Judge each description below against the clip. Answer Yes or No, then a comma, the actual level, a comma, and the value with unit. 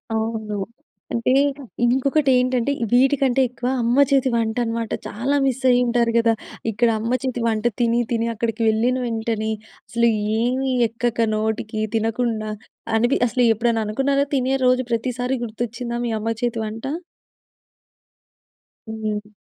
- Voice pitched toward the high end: Yes, high, 235 Hz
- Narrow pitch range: Yes, narrow, 2.1 semitones